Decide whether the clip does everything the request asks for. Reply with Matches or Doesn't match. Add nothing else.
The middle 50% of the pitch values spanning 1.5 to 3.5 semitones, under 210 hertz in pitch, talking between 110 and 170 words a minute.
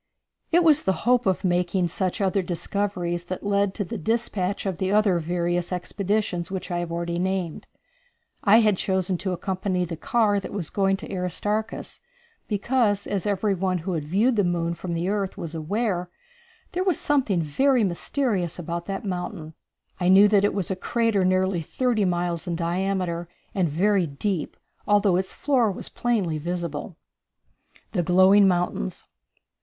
Matches